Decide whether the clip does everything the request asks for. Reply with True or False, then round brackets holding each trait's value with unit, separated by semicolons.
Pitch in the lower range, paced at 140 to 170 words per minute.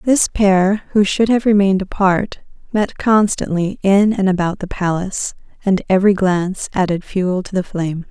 False (190 Hz; 165 wpm)